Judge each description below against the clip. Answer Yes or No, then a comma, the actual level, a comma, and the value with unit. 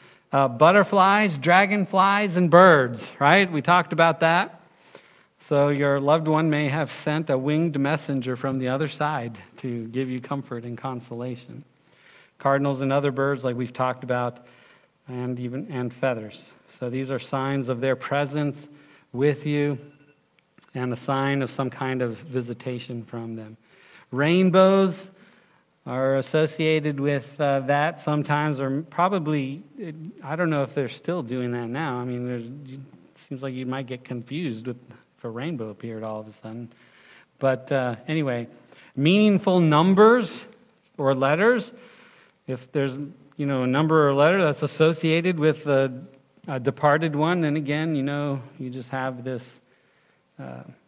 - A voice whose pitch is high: No, medium, 140 Hz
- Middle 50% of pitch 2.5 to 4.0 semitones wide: Yes, average, 3.6 semitones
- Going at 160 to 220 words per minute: No, average, 150 wpm